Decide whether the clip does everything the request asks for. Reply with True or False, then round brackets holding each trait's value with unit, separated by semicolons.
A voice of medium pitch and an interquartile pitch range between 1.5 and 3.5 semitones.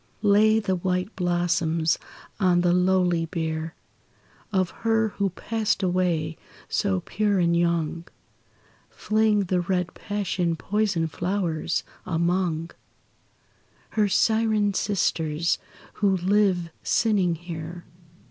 True (180 Hz; 3.2 semitones)